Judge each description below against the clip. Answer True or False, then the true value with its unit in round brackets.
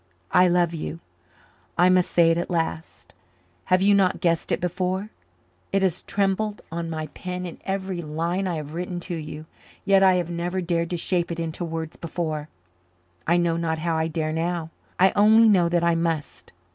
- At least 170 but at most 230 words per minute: True (190 wpm)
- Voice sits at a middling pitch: True (175 Hz)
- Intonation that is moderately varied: False (2.0 semitones)